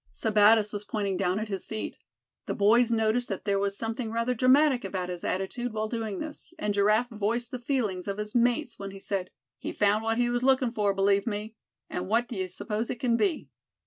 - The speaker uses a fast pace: Yes, fast, 210 wpm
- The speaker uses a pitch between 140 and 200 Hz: No, high, 215 Hz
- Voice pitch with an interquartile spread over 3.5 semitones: No, average, 3.1 semitones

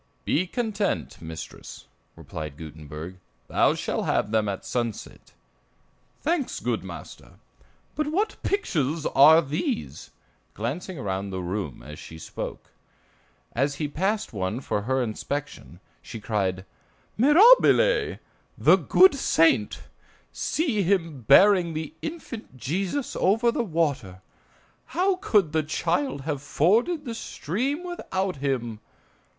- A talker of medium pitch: Yes, medium, 155 Hz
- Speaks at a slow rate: Yes, slow, 120 wpm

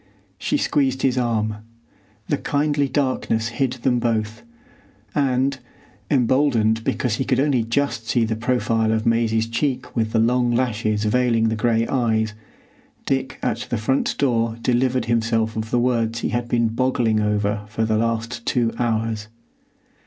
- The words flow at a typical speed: Yes, average, 155 wpm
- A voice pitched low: Yes, low, 115 Hz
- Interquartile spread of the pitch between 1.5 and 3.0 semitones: Yes, narrow, 2.4 semitones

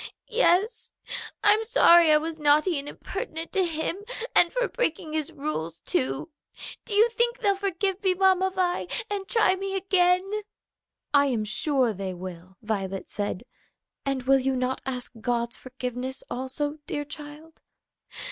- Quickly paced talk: No, average, 145 wpm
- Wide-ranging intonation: Yes, wide, 7.0 semitones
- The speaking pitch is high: Yes, very high, 310 Hz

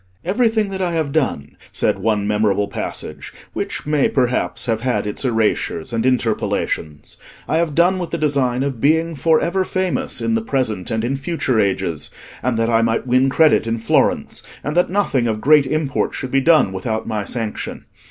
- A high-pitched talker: No, low, 130 Hz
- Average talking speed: Yes, average, 185 wpm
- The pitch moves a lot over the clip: Yes, wide, 6.3 semitones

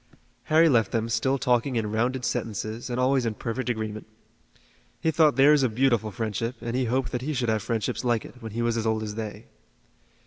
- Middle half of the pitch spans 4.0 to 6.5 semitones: No, average, 2.7 semitones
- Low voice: Yes, low, 120 Hz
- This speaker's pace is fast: Yes, fast, 210 wpm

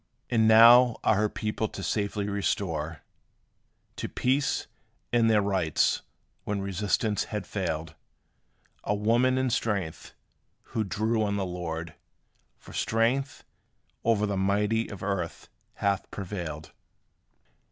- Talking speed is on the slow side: Yes, slow, 120 wpm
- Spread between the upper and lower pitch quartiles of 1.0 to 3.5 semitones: Yes, average, 2.9 semitones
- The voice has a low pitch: Yes, low, 105 Hz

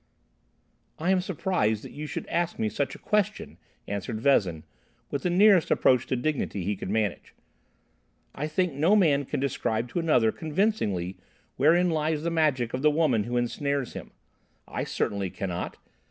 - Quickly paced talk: No, average, 165 wpm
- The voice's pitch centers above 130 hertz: Yes, medium, 140 Hz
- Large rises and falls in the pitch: Yes, wide, 7.1 semitones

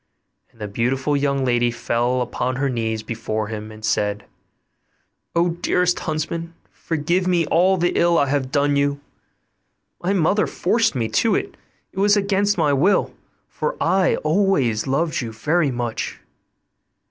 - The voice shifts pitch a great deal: Yes, wide, 6.6 semitones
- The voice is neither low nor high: Yes, medium, 145 Hz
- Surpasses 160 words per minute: No, average, 150 wpm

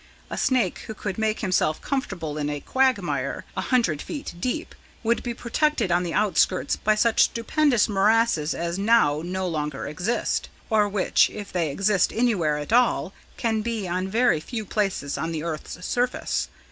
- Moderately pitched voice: No, high, 205 Hz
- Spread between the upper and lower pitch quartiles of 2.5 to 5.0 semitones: No, wide, 5.5 semitones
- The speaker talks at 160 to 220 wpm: Yes, average, 170 wpm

